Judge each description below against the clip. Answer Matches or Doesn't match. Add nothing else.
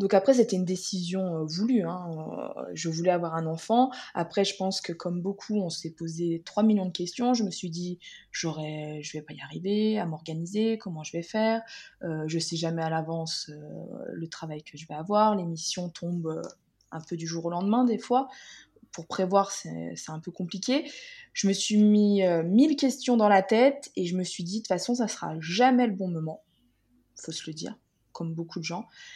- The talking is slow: Doesn't match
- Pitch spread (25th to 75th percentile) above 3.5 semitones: Matches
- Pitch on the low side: Doesn't match